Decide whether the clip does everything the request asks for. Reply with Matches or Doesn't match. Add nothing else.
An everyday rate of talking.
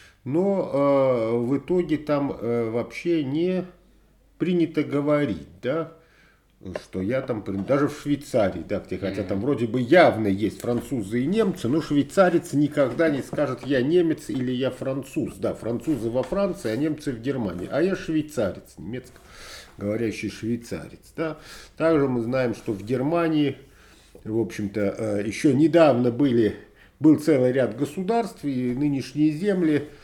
Matches